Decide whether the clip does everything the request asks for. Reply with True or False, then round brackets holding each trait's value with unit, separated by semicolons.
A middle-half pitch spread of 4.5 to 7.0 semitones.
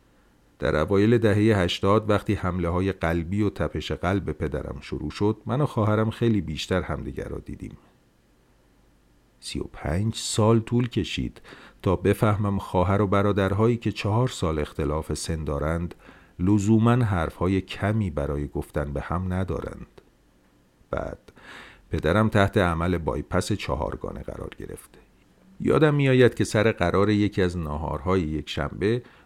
True (5.5 semitones)